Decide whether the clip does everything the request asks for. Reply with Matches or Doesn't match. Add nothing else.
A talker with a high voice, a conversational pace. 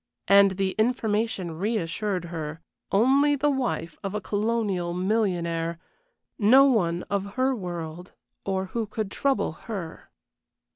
Doesn't match